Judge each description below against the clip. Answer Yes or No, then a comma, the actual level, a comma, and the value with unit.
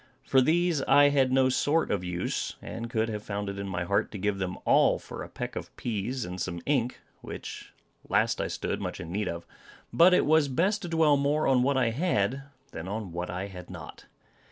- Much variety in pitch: Yes, wide, 6.7 semitones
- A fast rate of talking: Yes, fast, 220 wpm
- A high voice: No, low, 120 Hz